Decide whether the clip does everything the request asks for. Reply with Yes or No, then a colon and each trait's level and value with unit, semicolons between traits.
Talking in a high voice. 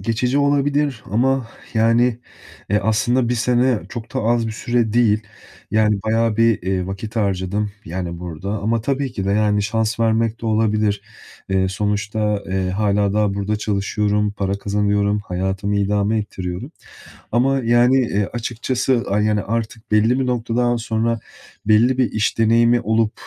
No: low, 110 Hz